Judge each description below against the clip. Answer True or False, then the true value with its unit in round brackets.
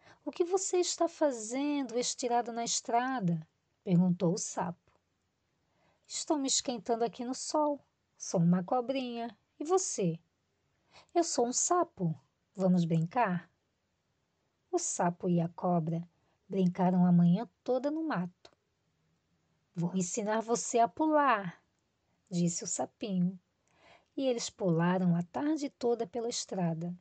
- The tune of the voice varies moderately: False (7.2 semitones)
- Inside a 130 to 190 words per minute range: False (120 wpm)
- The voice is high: True (225 Hz)